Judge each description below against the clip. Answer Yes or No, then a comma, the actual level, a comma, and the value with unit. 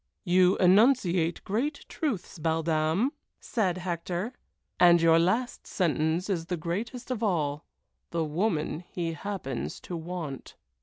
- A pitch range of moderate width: Yes, average, 3.7 semitones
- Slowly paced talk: Yes, slow, 130 wpm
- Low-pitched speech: No, medium, 175 Hz